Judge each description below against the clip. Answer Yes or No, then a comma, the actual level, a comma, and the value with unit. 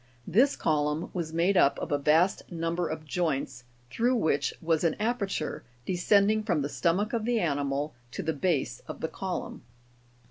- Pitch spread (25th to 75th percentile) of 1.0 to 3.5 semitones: No, average, 4.8 semitones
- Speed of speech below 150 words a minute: No, average, 170 wpm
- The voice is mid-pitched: Yes, medium, 165 Hz